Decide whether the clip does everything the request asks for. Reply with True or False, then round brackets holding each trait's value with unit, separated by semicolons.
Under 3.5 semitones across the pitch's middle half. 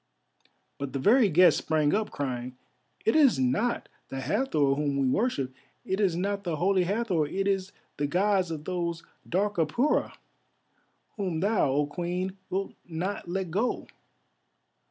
False (5.2 semitones)